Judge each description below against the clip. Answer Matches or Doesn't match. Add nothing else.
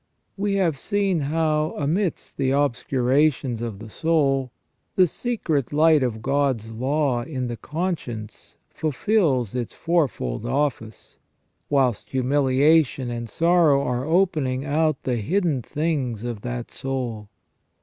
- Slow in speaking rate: Matches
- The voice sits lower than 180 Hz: Matches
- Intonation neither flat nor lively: Matches